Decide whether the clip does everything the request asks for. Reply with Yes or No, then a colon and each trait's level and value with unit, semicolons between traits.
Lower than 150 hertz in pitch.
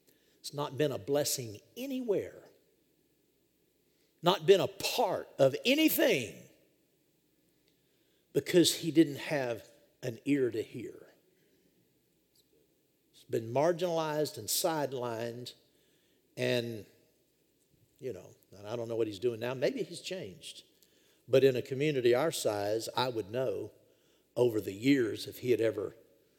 Yes: medium, 140 Hz